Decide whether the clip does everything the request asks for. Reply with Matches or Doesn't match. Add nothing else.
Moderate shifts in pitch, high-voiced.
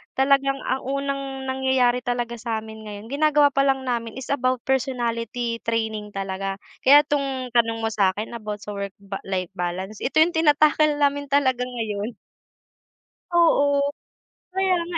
Matches